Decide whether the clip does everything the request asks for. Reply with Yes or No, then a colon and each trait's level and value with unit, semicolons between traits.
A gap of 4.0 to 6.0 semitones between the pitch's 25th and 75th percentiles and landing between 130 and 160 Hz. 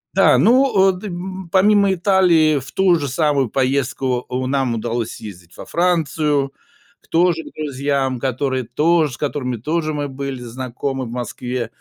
Yes: average, 4.9 semitones; medium, 140 Hz